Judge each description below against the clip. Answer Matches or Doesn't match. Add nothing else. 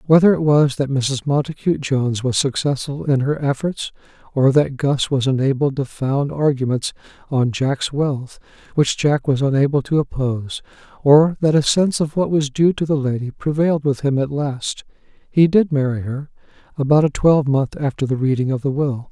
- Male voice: Matches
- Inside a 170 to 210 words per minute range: Matches